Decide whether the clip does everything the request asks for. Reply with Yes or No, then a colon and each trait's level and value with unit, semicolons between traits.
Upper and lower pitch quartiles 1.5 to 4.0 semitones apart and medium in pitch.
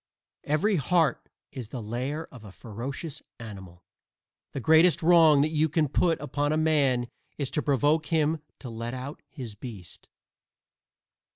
No: average, 4.7 semitones; medium, 145 Hz